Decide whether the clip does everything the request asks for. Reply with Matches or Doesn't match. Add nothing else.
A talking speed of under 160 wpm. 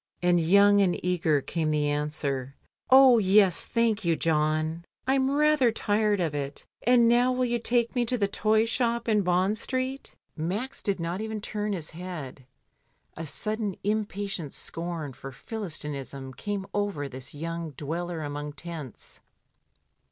Matches